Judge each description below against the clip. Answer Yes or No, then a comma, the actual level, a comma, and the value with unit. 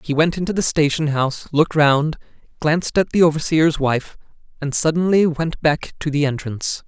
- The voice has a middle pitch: Yes, medium, 155 Hz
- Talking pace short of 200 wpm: Yes, average, 175 wpm